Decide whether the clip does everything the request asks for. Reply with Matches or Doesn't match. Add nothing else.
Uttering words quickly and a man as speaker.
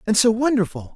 Doesn't match